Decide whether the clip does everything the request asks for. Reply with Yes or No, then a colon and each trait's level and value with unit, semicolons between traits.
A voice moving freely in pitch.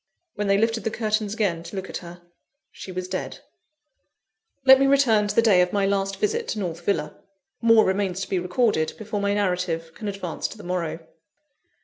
No: average, 3.3 semitones